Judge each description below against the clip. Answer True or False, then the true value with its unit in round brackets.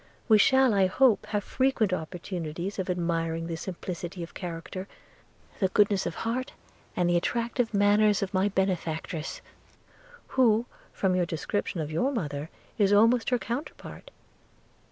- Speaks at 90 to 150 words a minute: True (140 wpm)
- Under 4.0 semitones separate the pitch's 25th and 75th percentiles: False (4.3 semitones)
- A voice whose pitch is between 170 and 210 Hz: True (190 Hz)